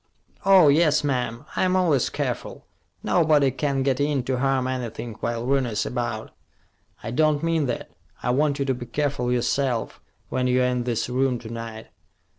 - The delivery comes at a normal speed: Yes, average, 165 wpm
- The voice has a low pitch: Yes, low, 130 Hz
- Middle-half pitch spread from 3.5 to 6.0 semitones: No, average, 3.0 semitones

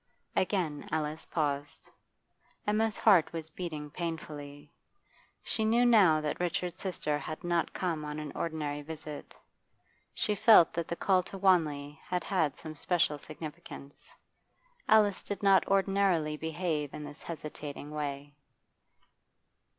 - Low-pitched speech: No, medium, 160 Hz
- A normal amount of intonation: Yes, average, 3.9 semitones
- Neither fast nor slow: No, slow, 125 wpm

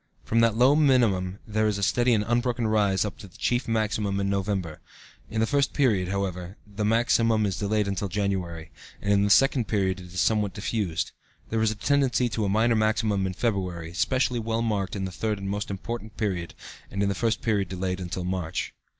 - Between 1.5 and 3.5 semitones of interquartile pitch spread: Yes, average, 2.9 semitones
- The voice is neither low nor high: No, low, 105 Hz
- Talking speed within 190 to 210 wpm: Yes, fast, 205 wpm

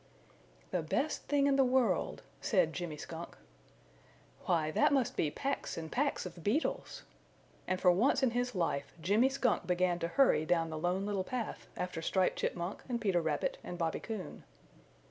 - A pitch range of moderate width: No, wide, 6.7 semitones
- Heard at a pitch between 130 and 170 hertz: No, medium, 185 Hz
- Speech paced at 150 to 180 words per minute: Yes, average, 170 wpm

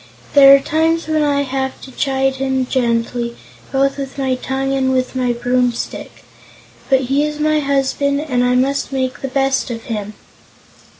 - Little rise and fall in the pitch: Yes, narrow, 1.7 semitones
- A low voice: No, very high, 270 Hz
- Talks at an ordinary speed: Yes, average, 170 wpm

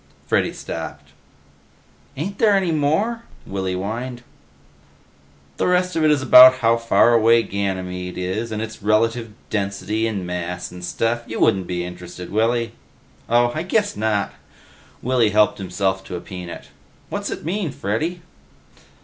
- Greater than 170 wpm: No, average, 145 wpm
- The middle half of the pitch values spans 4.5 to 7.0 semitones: Yes, average, 5.3 semitones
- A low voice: Yes, low, 110 Hz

